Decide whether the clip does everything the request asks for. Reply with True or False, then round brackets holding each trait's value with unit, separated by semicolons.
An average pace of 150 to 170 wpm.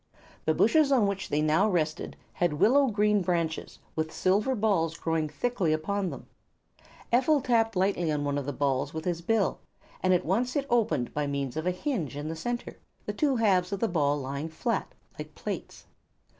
False (190 wpm)